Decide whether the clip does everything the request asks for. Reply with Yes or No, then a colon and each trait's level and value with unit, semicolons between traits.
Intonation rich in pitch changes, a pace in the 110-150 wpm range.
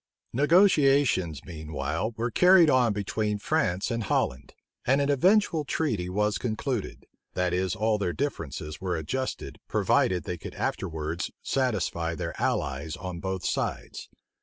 Yes: wide, 7.6 semitones; slow, 135 wpm